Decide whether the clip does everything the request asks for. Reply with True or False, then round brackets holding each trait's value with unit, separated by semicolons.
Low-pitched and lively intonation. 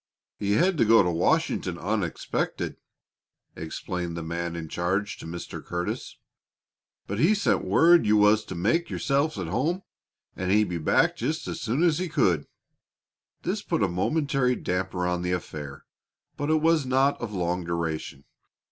True (100 Hz; 8.3 semitones)